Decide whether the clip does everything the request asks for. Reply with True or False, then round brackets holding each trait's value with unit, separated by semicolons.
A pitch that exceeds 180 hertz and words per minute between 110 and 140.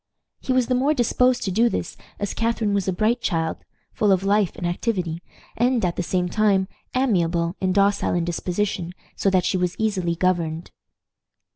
False (190 Hz; 180 wpm)